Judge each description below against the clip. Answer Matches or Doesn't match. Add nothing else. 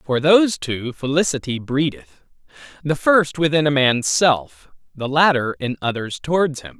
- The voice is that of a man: Matches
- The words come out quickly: Doesn't match